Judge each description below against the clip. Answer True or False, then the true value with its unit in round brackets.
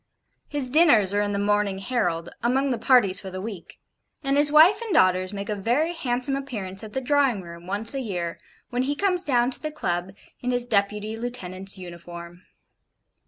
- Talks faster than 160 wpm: True (190 wpm)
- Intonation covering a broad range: True (5.9 semitones)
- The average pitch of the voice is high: True (220 Hz)